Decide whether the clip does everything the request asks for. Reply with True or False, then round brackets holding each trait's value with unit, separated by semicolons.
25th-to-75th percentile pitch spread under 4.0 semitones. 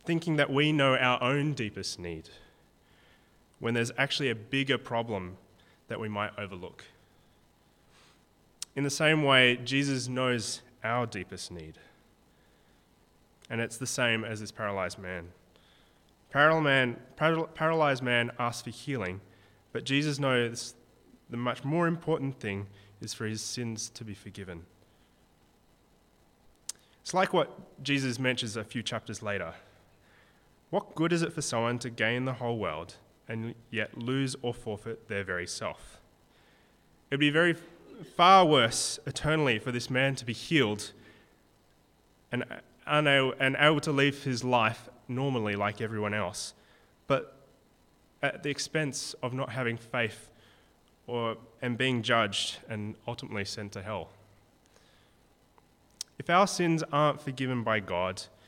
False (4.5 semitones)